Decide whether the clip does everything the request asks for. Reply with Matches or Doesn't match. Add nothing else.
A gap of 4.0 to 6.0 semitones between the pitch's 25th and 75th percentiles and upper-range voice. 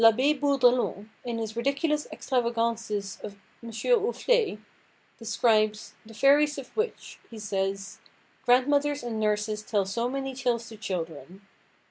Matches